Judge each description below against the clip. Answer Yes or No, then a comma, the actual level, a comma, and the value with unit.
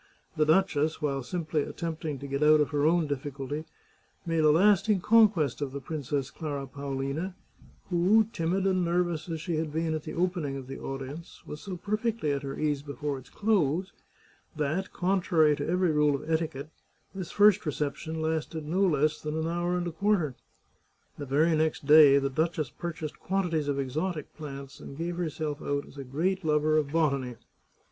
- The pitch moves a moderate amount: Yes, average, 3.4 semitones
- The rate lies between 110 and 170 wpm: No, average, 185 wpm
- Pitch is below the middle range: No, medium, 155 Hz